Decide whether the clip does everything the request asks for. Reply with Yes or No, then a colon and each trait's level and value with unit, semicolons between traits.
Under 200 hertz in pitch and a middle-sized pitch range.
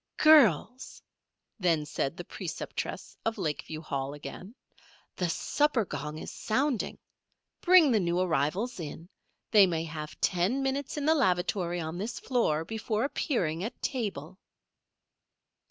No: medium, 185 Hz; wide, 7.3 semitones